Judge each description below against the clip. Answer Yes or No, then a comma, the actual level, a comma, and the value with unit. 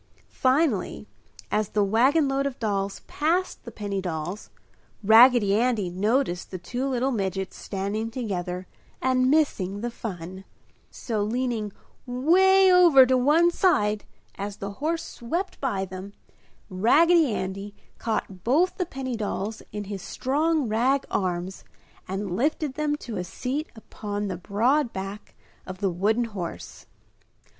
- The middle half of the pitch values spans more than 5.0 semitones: Yes, wide, 5.6 semitones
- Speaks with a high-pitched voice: Yes, high, 220 Hz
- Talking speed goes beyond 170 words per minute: No, slow, 135 wpm